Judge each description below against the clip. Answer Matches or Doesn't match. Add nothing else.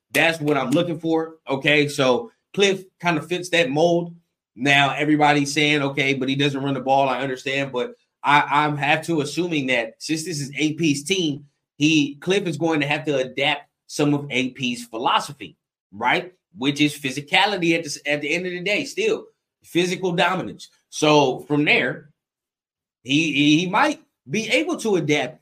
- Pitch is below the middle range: Doesn't match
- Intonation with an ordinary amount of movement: Matches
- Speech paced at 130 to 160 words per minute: Doesn't match